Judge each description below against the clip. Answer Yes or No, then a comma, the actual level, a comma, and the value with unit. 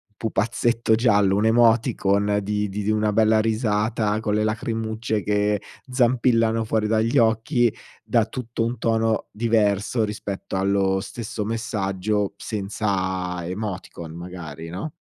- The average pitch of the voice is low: Yes, low, 110 Hz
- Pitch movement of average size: No, narrow, 2.1 semitones